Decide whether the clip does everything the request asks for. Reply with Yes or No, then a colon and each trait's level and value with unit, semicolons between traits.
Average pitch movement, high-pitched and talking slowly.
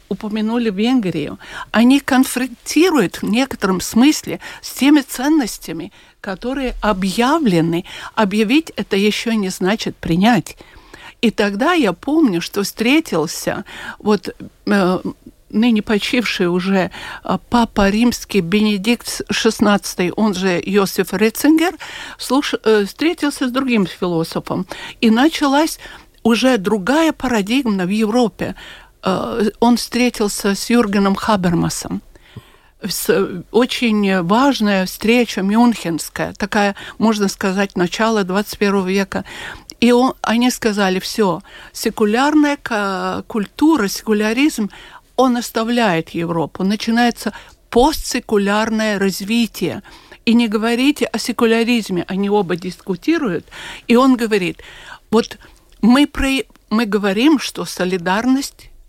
Yes: average, 3.6 semitones; high, 220 Hz; slow, 100 wpm